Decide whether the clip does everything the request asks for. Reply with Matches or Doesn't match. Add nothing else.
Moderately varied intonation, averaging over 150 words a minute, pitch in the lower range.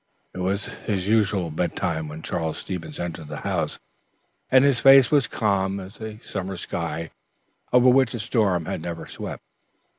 Matches